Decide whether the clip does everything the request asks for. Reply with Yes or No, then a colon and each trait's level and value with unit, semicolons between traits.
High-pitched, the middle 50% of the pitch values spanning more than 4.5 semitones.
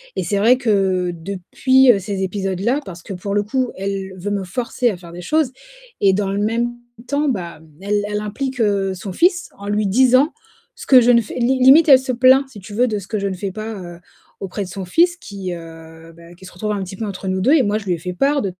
Yes: high, 205 Hz; average, 4.9 semitones